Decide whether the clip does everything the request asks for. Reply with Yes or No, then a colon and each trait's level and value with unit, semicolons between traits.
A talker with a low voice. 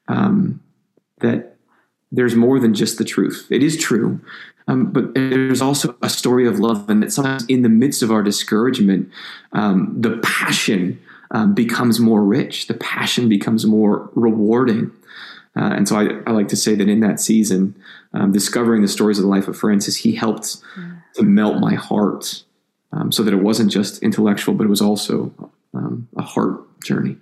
Yes: low, 110 Hz